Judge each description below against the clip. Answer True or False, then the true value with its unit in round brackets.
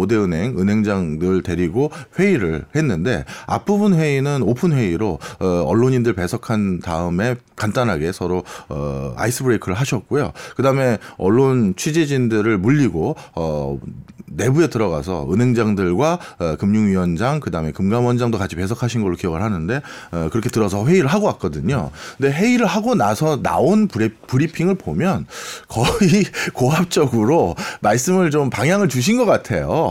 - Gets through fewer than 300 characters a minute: False (325 characters per minute)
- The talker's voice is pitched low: True (120 Hz)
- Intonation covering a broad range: True (8.2 semitones)